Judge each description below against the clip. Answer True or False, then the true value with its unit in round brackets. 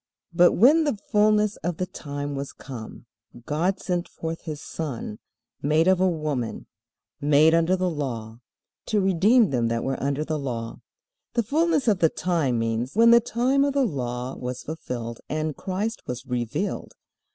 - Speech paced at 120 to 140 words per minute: False (165 wpm)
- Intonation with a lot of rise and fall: True (7.3 semitones)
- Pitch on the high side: False (160 Hz)